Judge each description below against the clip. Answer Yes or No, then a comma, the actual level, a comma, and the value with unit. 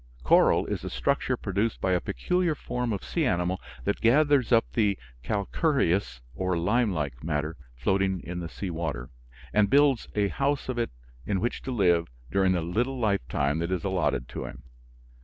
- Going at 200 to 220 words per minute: No, average, 175 wpm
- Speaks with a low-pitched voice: Yes, very low, 95 Hz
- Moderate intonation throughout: No, wide, 6.0 semitones